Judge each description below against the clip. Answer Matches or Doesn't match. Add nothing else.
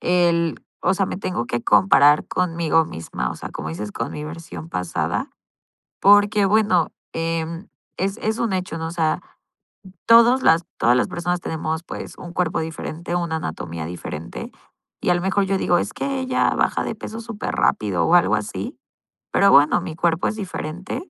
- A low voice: Doesn't match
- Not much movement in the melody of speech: Doesn't match